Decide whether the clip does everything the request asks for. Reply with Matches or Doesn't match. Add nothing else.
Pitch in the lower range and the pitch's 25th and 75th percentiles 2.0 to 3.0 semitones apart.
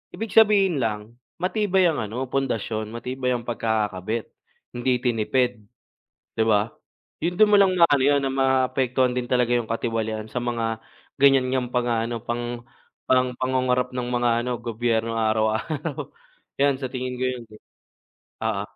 Matches